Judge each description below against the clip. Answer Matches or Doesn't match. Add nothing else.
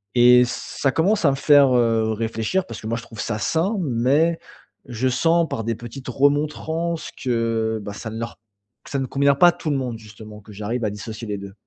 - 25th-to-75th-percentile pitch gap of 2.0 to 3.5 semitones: Doesn't match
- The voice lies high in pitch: Doesn't match